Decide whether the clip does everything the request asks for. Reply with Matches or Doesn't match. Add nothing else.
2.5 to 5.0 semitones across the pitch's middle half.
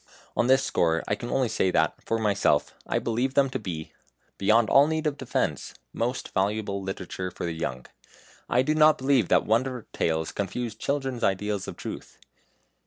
Doesn't match